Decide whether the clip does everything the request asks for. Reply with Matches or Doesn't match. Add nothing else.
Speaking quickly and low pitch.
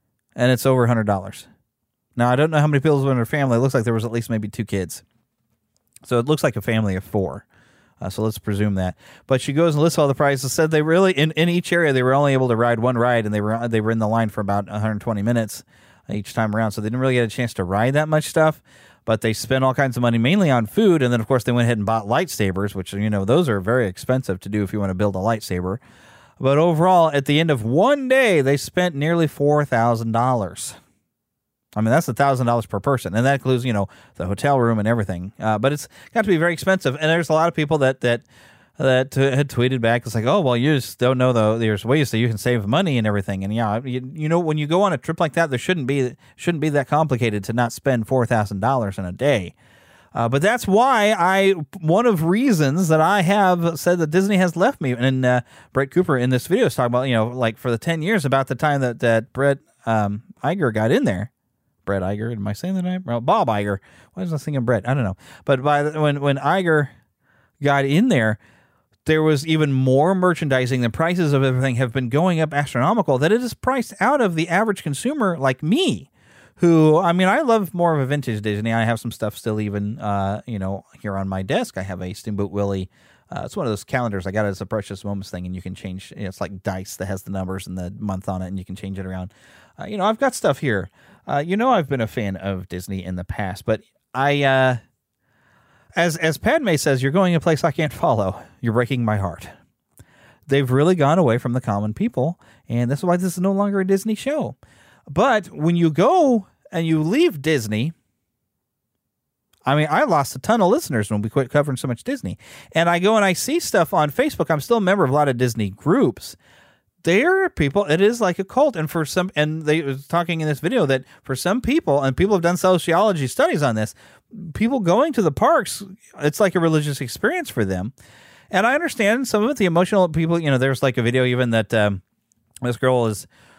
Matches